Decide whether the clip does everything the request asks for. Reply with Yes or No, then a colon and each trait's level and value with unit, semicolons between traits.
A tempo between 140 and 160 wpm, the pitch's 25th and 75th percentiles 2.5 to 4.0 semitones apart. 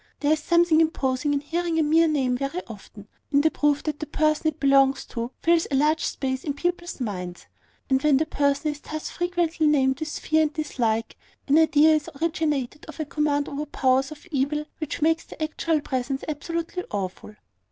No: average, 195 wpm; average, 2.8 semitones